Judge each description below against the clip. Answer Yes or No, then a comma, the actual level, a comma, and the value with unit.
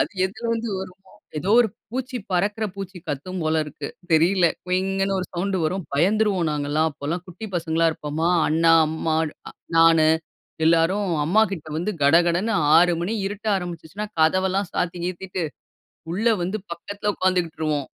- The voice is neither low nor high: Yes, medium, 180 Hz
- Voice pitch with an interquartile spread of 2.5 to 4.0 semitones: Yes, average, 3.2 semitones